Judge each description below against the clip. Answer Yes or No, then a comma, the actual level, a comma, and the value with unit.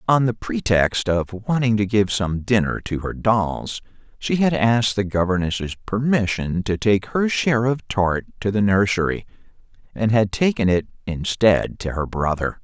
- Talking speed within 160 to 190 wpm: Yes, average, 165 wpm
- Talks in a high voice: No, low, 105 Hz